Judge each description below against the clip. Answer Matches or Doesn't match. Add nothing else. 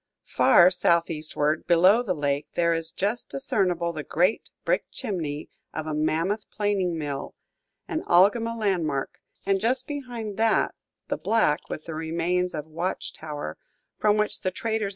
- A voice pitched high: Doesn't match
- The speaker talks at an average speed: Doesn't match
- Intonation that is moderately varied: Matches